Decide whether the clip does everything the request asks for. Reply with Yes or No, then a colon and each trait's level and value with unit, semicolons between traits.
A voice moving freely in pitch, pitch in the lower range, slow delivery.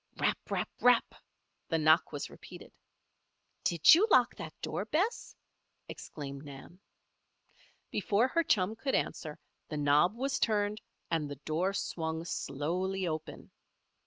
No: wide, 6.1 semitones; medium, 175 Hz; slow, 130 wpm